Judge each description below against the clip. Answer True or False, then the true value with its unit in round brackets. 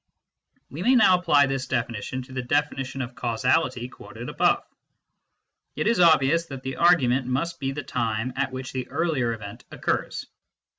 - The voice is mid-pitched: False (130 Hz)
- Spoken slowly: False (160 wpm)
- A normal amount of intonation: True (3.5 semitones)